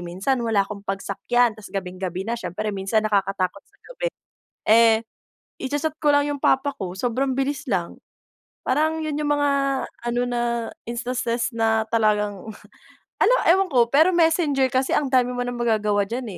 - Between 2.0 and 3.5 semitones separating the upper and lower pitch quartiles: No, average, 5.0 semitones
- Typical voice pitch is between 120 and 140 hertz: No, high, 240 Hz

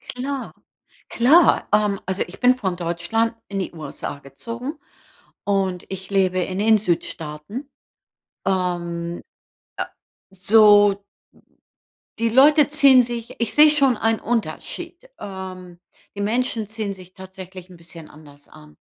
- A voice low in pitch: No, high, 195 Hz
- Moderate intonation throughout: Yes, average, 4.6 semitones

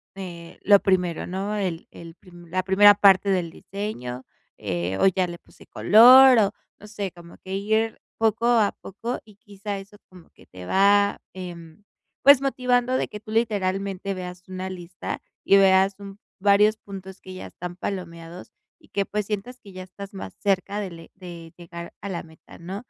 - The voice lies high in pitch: Yes, high, 195 Hz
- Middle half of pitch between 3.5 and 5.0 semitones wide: No, narrow, 2.6 semitones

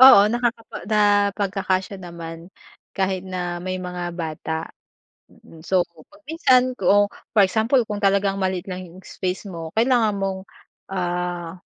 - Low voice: No, high, 190 Hz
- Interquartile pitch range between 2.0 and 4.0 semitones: Yes, average, 2.7 semitones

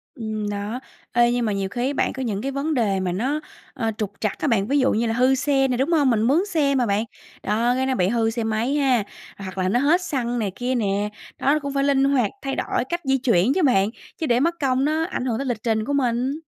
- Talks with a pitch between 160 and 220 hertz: No, high, 245 Hz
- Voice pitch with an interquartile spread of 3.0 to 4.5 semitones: Yes, average, 4.1 semitones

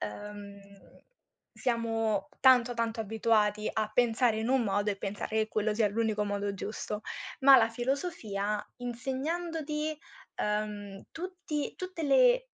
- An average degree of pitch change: Yes, average, 4.3 semitones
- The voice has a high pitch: Yes, high, 225 Hz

